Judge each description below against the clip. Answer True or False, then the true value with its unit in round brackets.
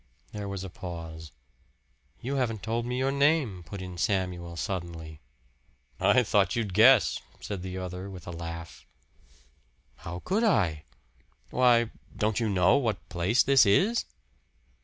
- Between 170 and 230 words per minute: False (140 wpm)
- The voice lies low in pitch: True (100 Hz)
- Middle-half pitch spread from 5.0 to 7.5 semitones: True (5.3 semitones)